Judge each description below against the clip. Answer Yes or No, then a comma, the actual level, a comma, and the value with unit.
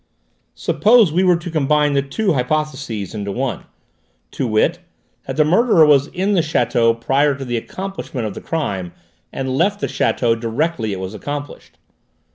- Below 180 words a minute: Yes, average, 165 wpm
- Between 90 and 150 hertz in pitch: Yes, medium, 140 Hz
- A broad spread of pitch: Yes, wide, 6.2 semitones